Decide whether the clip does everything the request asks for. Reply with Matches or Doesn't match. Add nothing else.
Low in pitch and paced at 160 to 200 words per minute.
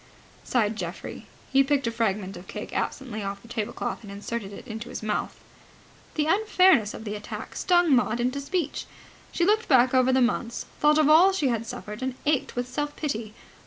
Doesn't match